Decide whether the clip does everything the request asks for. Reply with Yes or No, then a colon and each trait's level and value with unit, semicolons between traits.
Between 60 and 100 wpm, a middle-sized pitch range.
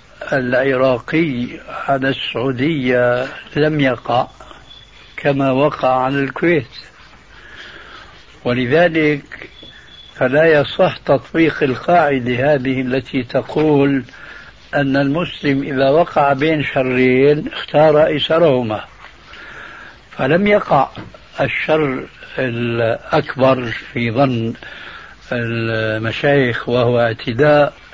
Yes: average, 75 wpm; average, 3.0 semitones